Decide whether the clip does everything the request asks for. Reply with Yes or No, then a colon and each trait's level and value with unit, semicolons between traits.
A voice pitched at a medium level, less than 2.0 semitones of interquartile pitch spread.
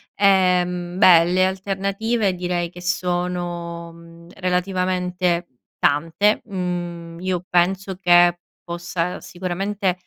Yes: medium, 180 Hz; narrow, 1.3 semitones